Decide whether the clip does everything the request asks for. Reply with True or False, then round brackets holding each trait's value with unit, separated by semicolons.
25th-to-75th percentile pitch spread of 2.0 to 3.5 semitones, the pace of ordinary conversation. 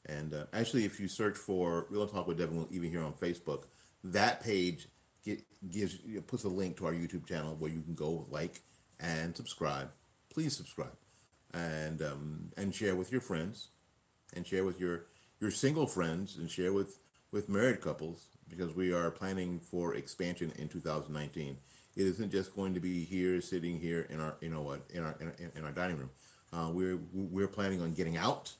True (2.8 semitones; 195 wpm)